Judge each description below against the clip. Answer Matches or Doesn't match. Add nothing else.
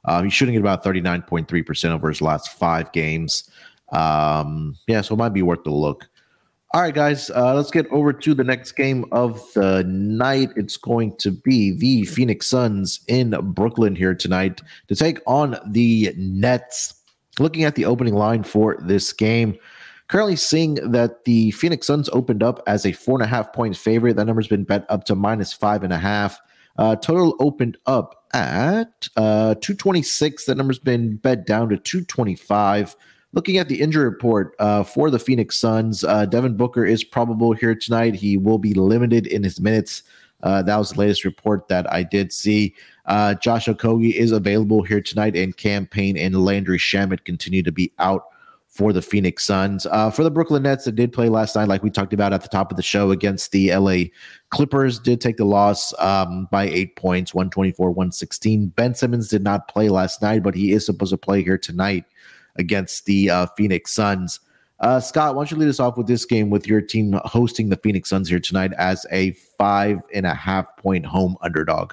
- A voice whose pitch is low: Matches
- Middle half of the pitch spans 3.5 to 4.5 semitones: Matches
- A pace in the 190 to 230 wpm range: Matches